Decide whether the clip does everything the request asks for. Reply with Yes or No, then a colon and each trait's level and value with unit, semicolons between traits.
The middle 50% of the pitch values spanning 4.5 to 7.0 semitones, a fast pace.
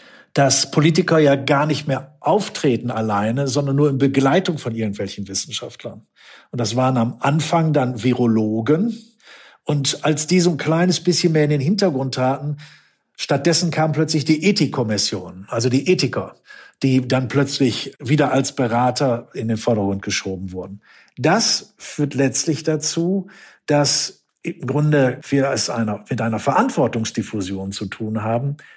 No: average, 5.0 semitones; average, 140 wpm